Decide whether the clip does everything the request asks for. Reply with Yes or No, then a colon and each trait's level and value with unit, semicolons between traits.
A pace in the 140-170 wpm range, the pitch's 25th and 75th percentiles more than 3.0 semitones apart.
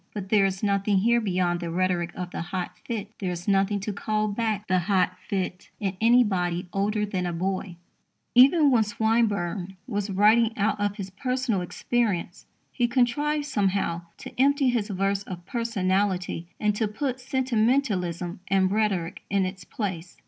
Yes: average, 165 wpm; average, 3.4 semitones